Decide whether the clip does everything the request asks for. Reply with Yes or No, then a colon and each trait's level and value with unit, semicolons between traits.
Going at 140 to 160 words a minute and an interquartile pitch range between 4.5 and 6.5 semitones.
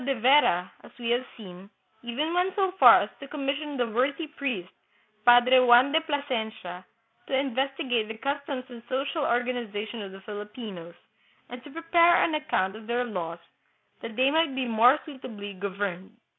No: average, 170 wpm; average, 4.8 semitones